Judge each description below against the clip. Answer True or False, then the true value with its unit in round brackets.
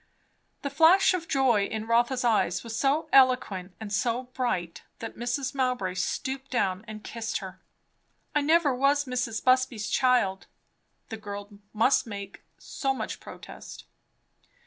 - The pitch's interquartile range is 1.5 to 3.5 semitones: False (4.5 semitones)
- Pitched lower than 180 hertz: False (240 Hz)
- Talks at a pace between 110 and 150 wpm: True (140 wpm)